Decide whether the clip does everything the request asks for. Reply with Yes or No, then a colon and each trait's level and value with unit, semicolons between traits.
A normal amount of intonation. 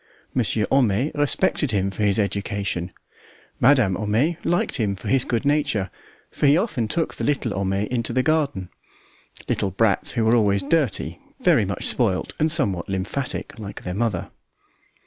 No: wide, 6.0 semitones